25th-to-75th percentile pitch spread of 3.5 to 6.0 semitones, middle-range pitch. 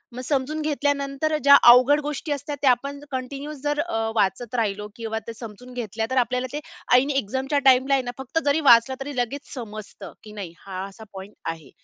No: average, 4.1 semitones; very high, 255 Hz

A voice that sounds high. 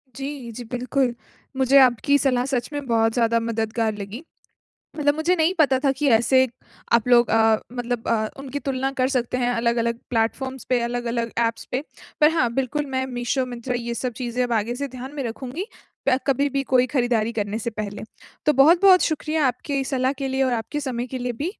Yes: very high, 250 Hz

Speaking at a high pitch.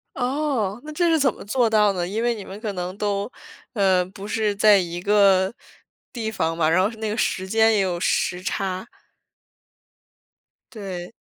Yes: high, 200 Hz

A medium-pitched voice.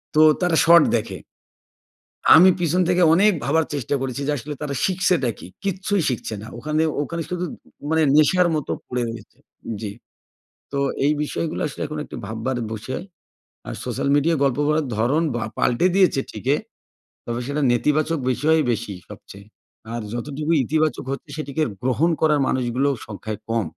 Yes: medium, 145 Hz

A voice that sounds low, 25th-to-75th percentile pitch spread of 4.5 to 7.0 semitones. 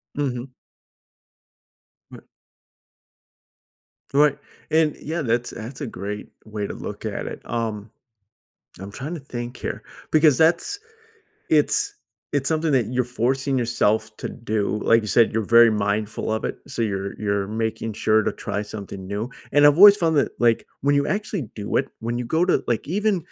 Yes: low, 120 Hz; average, 5.2 semitones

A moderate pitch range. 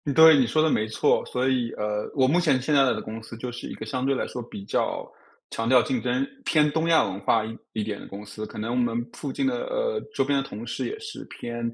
No: wide, 5.7 semitones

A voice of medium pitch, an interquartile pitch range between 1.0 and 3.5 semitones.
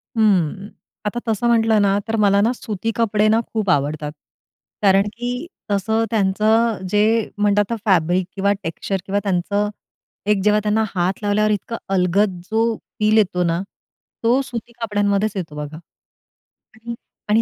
No: high, 205 Hz; narrow, 2.6 semitones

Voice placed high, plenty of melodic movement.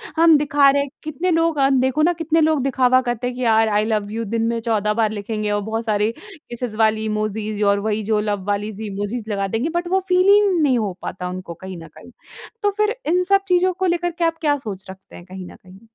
Yes: high, 225 Hz; wide, 6.9 semitones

